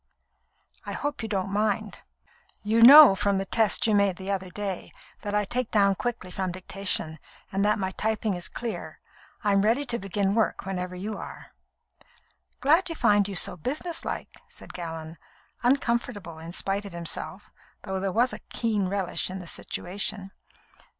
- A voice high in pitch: Yes, high, 200 Hz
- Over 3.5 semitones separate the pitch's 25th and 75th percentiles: No, average, 2.9 semitones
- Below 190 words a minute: Yes, average, 170 wpm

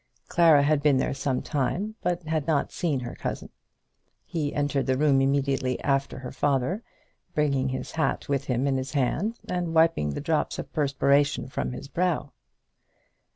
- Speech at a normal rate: Yes, average, 165 wpm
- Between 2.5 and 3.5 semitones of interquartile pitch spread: Yes, average, 3.0 semitones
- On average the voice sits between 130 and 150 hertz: Yes, medium, 140 Hz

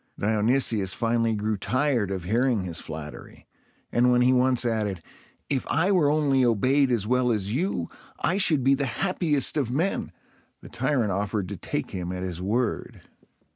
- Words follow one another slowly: No, average, 170 wpm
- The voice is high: No, low, 120 Hz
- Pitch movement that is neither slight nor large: Yes, average, 4.9 semitones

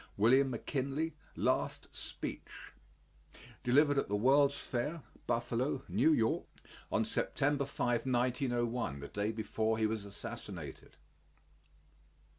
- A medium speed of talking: No, slow, 100 wpm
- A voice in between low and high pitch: No, low, 120 Hz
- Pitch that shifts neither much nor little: Yes, average, 3.7 semitones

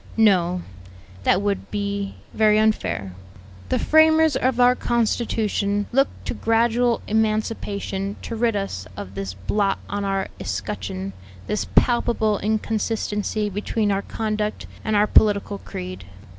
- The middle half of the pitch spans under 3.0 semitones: Yes, narrow, 2.4 semitones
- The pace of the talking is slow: Yes, slow, 125 wpm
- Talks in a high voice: Yes, high, 210 Hz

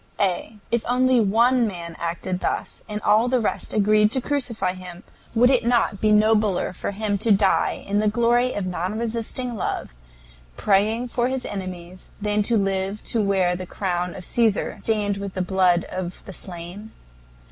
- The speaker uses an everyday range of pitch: Yes, average, 3.7 semitones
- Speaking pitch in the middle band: No, high, 210 Hz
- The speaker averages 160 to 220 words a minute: Yes, average, 175 wpm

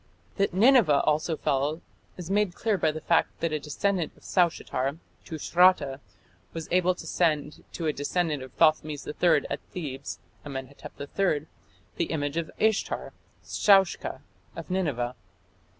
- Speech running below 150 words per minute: Yes, average, 140 wpm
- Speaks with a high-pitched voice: No, medium, 160 Hz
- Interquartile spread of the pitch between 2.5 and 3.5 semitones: No, average, 3.9 semitones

